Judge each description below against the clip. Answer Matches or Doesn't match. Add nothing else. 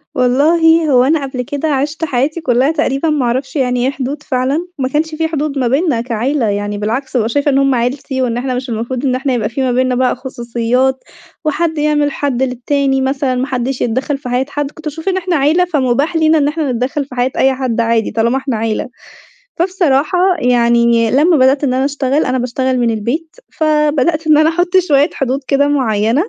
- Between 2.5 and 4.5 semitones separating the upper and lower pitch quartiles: Matches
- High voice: Matches